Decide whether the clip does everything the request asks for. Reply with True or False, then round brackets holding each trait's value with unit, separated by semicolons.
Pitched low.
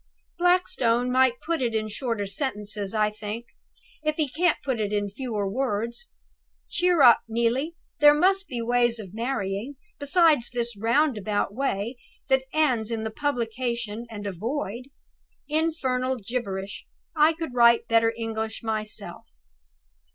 False (235 Hz)